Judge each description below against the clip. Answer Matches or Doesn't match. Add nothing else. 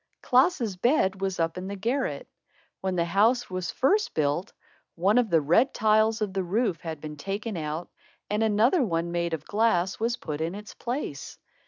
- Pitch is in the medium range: Doesn't match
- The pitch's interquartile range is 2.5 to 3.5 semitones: Doesn't match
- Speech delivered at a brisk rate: Doesn't match